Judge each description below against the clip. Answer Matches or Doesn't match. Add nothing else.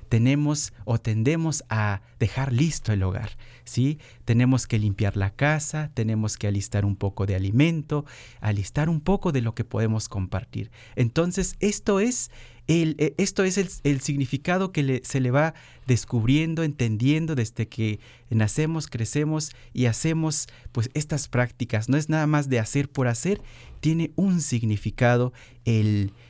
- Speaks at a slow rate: Doesn't match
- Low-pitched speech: Matches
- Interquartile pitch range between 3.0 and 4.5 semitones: Doesn't match